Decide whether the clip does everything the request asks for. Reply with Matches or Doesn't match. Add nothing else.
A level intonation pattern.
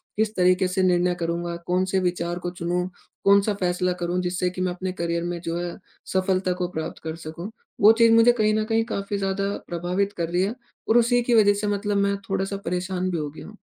Matches